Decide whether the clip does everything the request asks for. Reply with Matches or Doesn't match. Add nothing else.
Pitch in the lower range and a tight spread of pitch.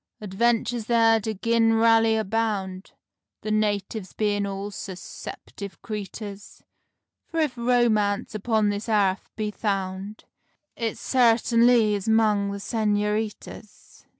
Doesn't match